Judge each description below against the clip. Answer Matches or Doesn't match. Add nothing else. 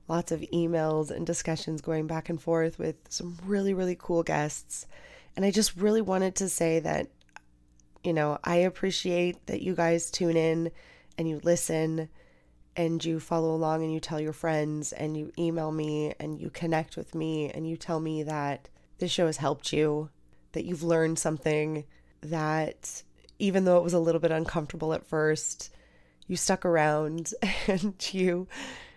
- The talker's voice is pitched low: Doesn't match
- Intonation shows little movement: Matches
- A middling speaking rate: Matches